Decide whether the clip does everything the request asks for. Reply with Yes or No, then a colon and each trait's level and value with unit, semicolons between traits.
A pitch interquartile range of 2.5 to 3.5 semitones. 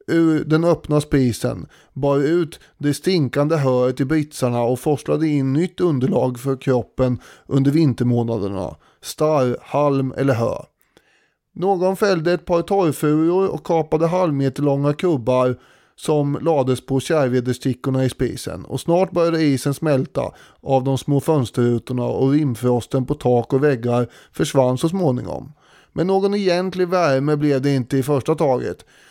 No: average, 3.9 semitones